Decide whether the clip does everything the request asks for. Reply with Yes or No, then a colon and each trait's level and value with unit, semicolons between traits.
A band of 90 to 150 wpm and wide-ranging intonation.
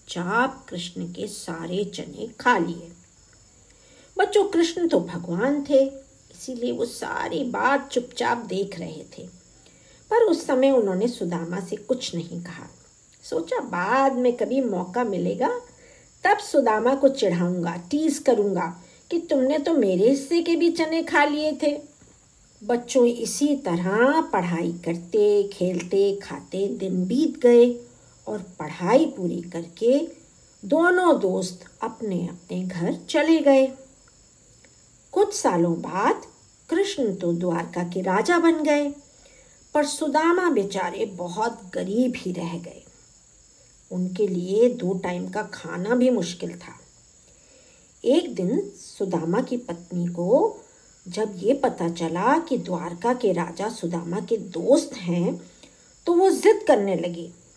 Yes: average, 130 wpm; wide, 8.4 semitones